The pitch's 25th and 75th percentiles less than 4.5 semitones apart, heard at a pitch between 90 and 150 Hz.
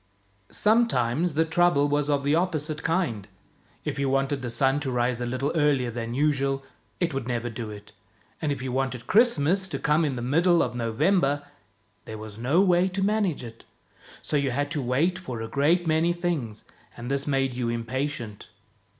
No: average, 5.0 semitones; medium, 140 Hz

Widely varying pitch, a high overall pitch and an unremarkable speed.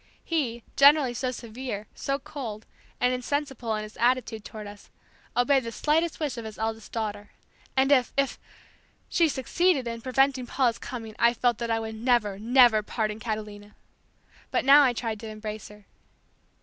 No: average, 3.4 semitones; high, 235 Hz; average, 165 wpm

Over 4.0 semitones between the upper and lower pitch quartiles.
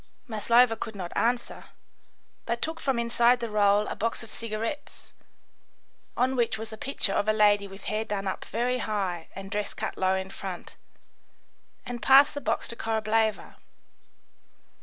No: narrow, 2.6 semitones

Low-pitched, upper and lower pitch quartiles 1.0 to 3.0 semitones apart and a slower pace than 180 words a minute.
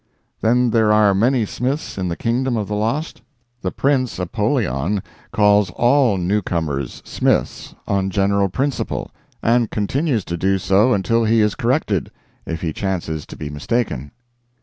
No: low, 105 Hz; average, 4.4 semitones; average, 150 wpm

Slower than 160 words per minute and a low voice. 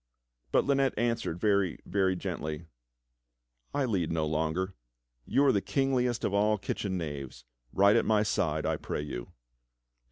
Yes: average, 150 wpm; very low, 95 Hz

